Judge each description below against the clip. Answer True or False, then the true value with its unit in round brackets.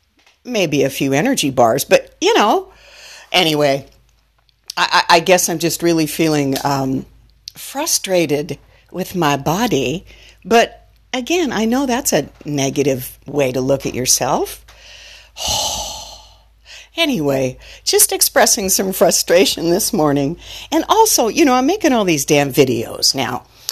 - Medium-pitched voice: True (170 Hz)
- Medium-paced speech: False (130 wpm)